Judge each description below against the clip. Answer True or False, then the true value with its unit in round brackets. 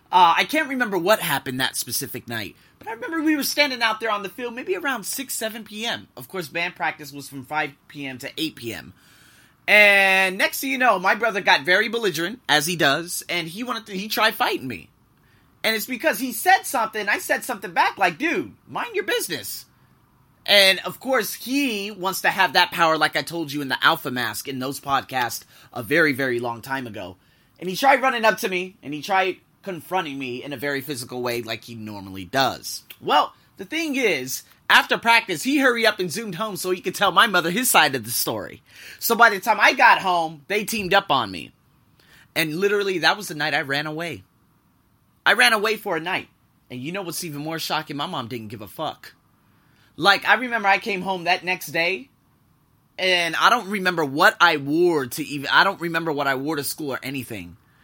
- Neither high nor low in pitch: True (180 Hz)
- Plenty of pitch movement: True (7.3 semitones)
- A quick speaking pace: True (220 wpm)